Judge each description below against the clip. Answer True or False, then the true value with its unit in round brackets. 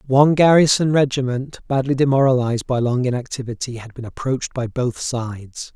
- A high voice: False (130 Hz)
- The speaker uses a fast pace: False (145 wpm)